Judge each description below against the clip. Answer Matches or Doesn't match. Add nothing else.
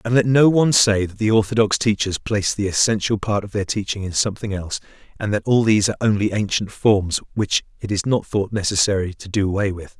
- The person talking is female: Doesn't match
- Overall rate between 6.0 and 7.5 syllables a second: Matches